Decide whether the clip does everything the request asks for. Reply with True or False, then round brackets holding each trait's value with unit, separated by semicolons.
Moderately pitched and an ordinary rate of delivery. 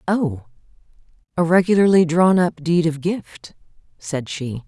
False (165 Hz; 130 wpm)